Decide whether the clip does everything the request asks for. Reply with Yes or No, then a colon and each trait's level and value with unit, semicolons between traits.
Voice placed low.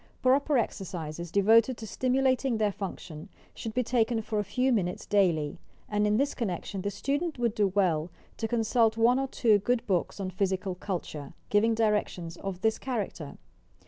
No: high, 210 Hz